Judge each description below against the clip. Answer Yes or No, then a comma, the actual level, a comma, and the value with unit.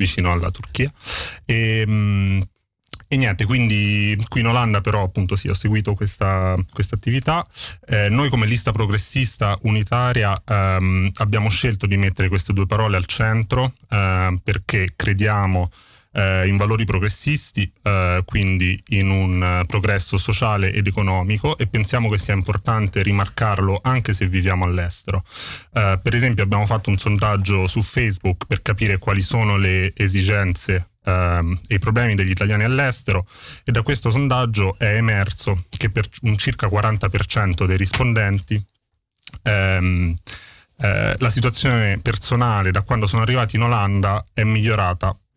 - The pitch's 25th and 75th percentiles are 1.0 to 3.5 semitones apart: Yes, average, 2.7 semitones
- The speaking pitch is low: Yes, low, 105 Hz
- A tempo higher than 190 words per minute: No, average, 145 wpm